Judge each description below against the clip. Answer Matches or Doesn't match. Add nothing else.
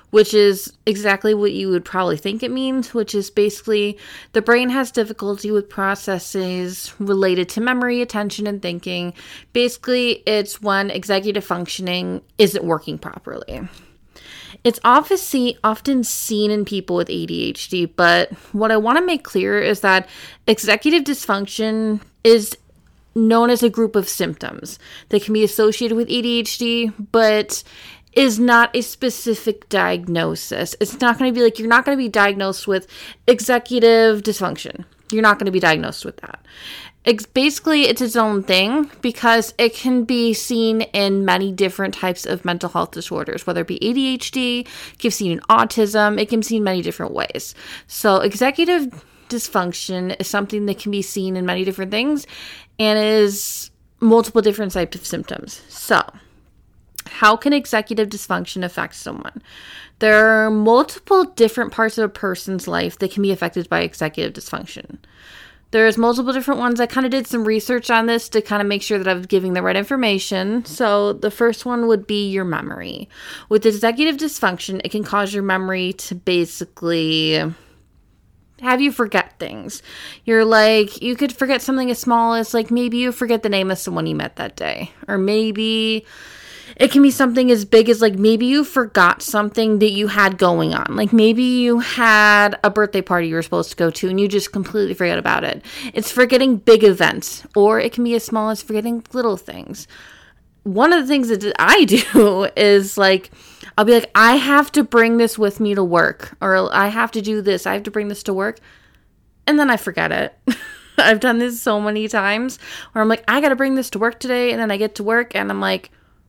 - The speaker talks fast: Doesn't match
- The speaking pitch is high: Matches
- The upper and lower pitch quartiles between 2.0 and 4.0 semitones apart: Matches